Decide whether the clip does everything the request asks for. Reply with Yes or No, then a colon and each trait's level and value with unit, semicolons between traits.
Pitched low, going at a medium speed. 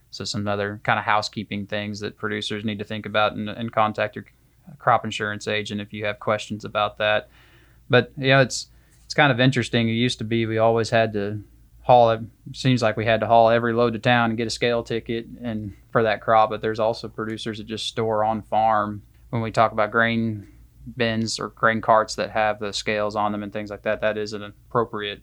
No: low, 110 Hz; fast, 225 wpm